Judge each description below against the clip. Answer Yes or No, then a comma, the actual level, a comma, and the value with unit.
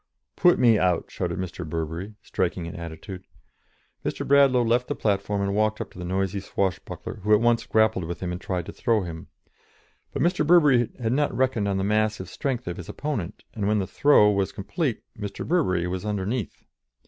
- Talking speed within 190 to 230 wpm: Yes, average, 195 wpm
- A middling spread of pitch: Yes, average, 4.4 semitones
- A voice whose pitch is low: Yes, low, 105 Hz